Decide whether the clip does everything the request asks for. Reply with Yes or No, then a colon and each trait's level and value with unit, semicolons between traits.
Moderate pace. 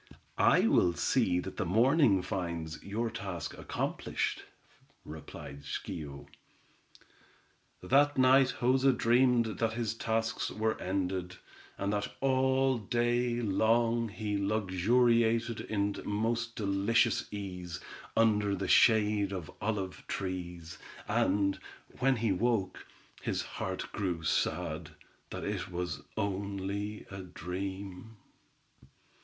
No: slow, 105 wpm